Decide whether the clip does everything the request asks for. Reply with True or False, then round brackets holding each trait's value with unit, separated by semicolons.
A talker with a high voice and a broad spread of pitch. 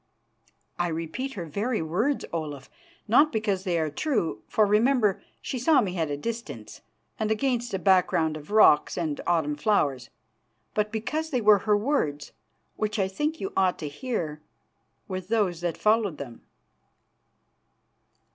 True (200 Hz; 6.0 semitones)